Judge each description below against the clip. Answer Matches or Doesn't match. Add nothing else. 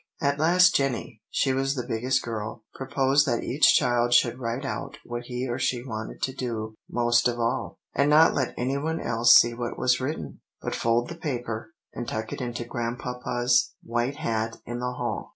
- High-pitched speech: Doesn't match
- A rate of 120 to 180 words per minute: Doesn't match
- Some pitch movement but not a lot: Doesn't match